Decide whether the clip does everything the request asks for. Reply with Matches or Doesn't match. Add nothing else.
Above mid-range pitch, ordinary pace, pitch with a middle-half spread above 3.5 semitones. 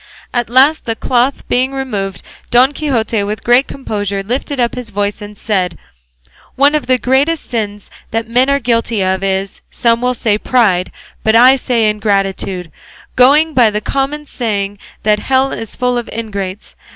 Matches